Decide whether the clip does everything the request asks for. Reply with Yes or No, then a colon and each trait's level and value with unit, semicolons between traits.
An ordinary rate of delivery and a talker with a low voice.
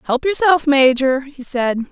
No: average, 155 wpm; very high, 275 Hz